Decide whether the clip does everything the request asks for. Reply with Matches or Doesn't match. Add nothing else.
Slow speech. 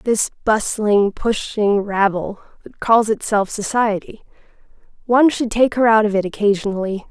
Matches